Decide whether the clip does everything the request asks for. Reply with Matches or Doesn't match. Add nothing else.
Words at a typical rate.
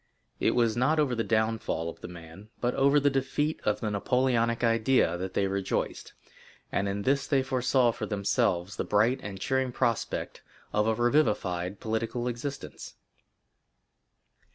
Matches